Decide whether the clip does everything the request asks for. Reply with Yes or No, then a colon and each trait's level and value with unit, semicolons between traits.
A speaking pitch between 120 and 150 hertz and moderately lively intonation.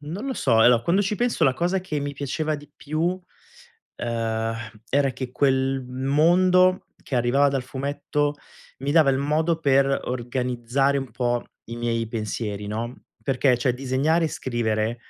Yes: low, 135 Hz; average, 3.8 semitones